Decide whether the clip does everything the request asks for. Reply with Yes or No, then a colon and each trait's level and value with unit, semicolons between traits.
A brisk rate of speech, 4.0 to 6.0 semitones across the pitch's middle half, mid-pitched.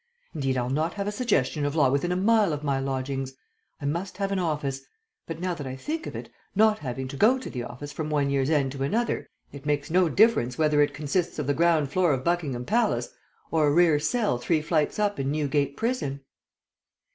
Yes: fast, 220 wpm; average, 4.7 semitones; medium, 150 Hz